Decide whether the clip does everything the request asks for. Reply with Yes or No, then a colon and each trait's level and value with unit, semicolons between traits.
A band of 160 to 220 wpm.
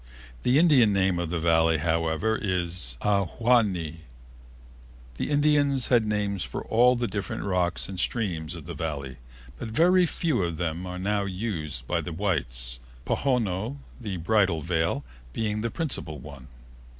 No: average, 150 wpm